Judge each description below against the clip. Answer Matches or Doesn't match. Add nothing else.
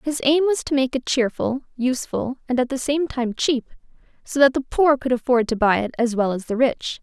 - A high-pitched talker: Matches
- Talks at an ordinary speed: Doesn't match